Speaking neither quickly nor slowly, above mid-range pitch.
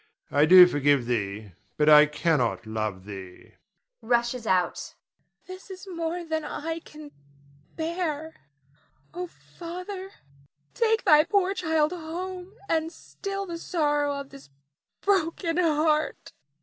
No: slow, 125 wpm; very high, 315 Hz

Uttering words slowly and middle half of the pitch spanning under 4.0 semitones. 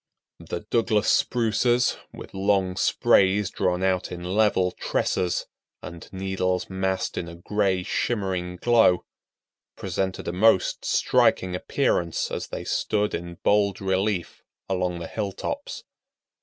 Yes: slow, 120 wpm; narrow, 2.4 semitones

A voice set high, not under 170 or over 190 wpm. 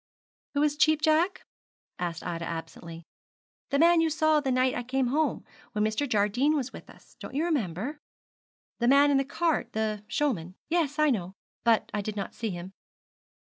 Yes: very high, 255 Hz; average, 180 wpm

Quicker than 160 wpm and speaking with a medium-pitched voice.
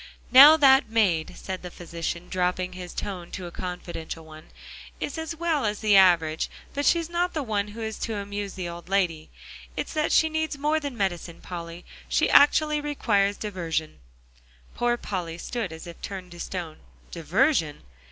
No: average, 170 wpm; high, 195 Hz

